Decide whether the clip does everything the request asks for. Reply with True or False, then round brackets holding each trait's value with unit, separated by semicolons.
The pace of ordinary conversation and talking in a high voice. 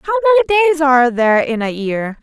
False (215 wpm; 295 Hz)